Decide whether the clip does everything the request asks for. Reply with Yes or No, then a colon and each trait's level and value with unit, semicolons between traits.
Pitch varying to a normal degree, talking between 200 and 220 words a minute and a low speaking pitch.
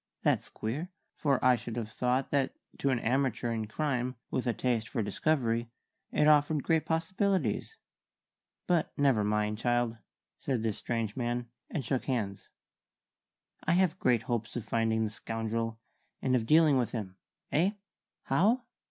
No: average, 4.2 semitones; average, 150 wpm; low, 125 Hz